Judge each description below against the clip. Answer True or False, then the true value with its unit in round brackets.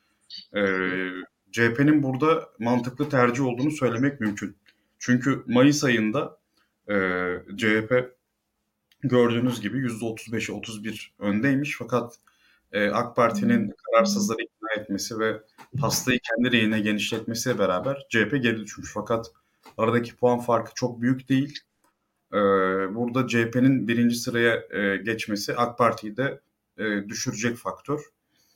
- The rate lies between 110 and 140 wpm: True (120 wpm)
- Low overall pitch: True (115 Hz)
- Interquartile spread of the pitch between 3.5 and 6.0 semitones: False (2.9 semitones)